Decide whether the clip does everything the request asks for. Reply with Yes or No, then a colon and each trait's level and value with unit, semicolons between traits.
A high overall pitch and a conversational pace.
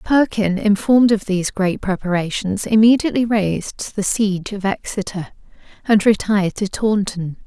No: high, 205 Hz; slow, 130 wpm